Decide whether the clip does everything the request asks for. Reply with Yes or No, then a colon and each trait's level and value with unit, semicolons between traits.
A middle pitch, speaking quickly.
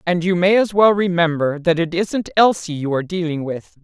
Yes: medium, 175 Hz; fast, 220 wpm